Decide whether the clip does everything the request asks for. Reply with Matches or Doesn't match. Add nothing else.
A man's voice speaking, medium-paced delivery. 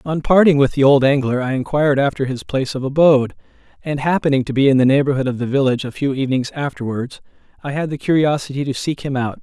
Doesn't match